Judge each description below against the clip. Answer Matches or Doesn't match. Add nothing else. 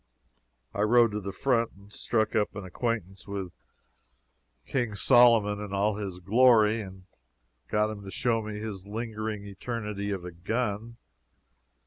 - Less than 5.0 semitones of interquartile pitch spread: Matches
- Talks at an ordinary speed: Matches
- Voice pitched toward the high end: Doesn't match